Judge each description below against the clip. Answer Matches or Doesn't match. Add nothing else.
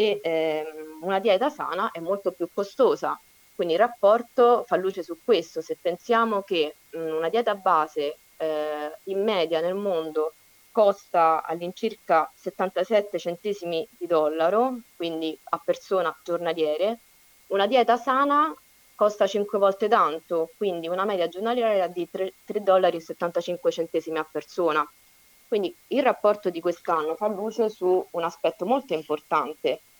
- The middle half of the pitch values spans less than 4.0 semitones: Doesn't match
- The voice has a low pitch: Doesn't match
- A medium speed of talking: Matches